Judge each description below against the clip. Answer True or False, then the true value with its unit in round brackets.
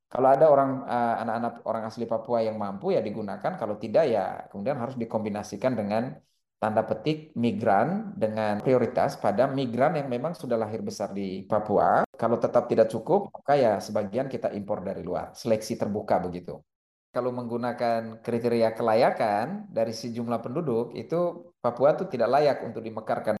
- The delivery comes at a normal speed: False (155 wpm)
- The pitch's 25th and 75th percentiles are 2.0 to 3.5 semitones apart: True (2.7 semitones)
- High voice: False (120 Hz)